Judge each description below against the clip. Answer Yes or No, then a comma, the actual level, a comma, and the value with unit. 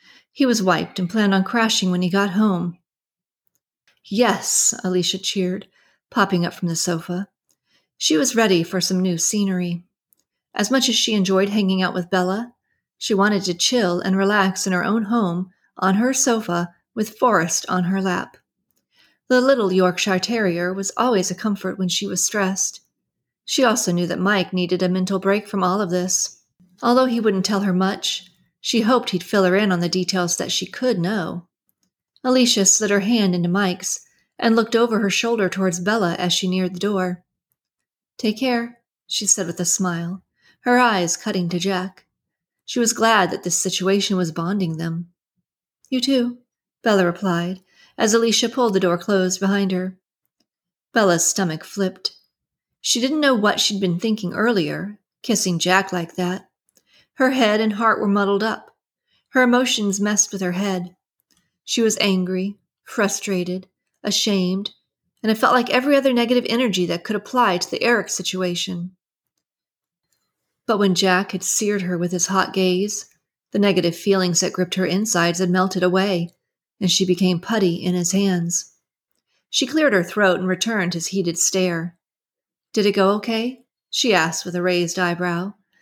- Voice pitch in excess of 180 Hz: Yes, high, 190 Hz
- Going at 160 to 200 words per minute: Yes, average, 170 wpm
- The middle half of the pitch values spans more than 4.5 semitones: No, average, 3.1 semitones